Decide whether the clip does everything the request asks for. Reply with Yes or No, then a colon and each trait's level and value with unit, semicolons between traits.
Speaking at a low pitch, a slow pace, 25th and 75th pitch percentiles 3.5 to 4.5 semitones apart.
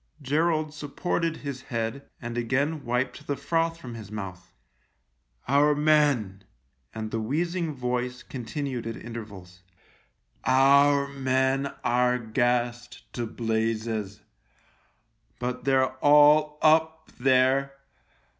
Yes: low, 130 Hz; slow, 110 wpm; average, 4.0 semitones